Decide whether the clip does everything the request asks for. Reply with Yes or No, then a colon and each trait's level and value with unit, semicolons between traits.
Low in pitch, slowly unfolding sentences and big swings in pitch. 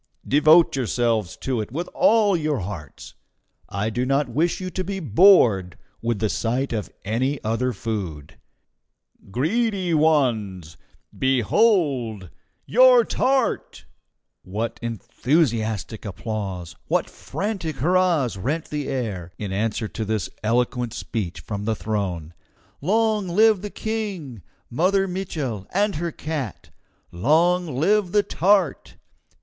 Yes: low, 130 Hz; slow, 120 wpm; wide, 8.7 semitones